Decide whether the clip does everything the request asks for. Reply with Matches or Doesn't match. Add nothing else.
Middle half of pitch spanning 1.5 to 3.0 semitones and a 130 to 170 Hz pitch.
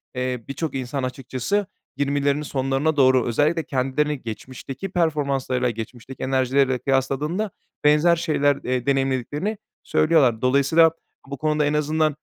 Matches